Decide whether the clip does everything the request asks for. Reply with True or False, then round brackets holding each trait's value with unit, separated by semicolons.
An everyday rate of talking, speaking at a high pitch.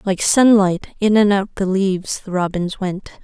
True (185 wpm; 195 Hz)